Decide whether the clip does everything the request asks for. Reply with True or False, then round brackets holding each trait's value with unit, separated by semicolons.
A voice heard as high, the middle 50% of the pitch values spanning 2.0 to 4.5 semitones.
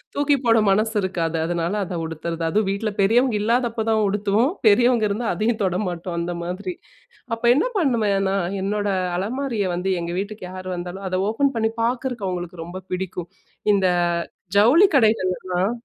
True (200 Hz; 3.9 semitones)